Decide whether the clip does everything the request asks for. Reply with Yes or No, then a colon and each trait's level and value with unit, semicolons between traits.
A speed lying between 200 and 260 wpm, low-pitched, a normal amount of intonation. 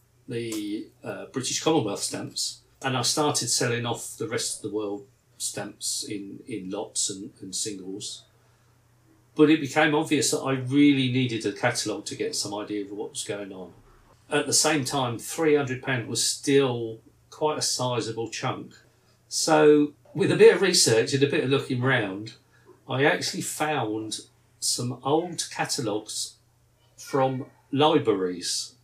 No: average, 150 wpm; low, 125 Hz; average, 4.1 semitones